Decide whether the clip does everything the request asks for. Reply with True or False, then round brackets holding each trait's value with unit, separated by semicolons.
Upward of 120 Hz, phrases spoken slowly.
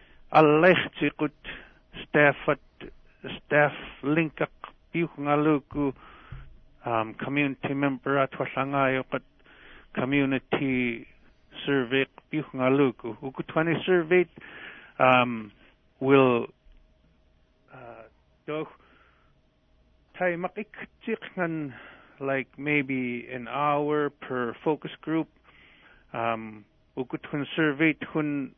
True (140 Hz; 90 wpm)